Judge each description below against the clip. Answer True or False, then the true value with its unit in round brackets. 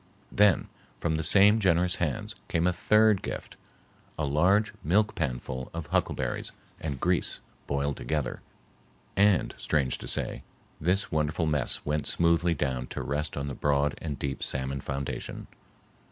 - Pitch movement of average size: True (4.3 semitones)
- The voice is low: True (75 Hz)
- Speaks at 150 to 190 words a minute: False (140 wpm)